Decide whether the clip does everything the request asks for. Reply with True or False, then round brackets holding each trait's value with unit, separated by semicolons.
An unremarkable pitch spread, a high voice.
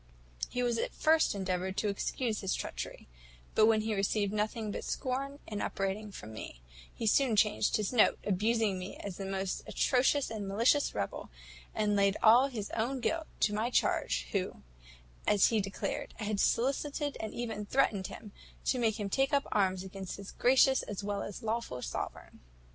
True (3.5 semitones; 215 Hz)